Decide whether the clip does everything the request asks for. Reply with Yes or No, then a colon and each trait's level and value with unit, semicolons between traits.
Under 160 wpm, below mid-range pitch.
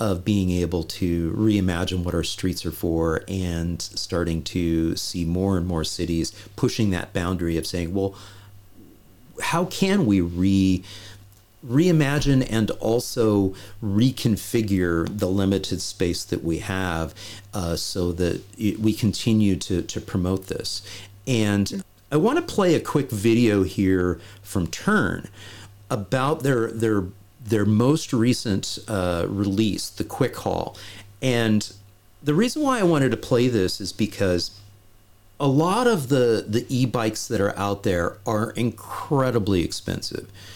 Yes: average, 140 wpm; low, 100 Hz